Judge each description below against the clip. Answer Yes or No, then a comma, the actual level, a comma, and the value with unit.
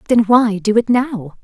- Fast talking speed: Yes, fast, 210 wpm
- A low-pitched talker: No, high, 220 Hz